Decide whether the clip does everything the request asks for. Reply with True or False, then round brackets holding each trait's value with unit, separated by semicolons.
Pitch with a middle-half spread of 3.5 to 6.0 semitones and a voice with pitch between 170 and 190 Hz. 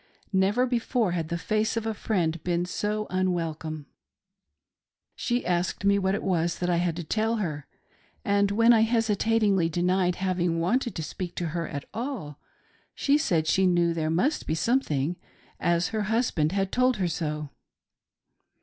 True (4.5 semitones; 185 Hz)